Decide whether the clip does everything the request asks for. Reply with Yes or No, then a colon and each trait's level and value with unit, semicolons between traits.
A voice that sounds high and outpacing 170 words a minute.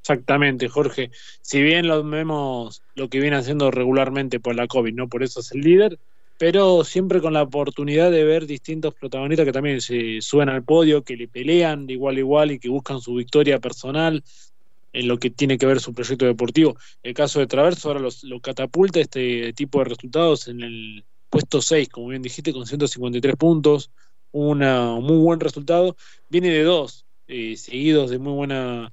No: medium, 140 Hz; average, 185 wpm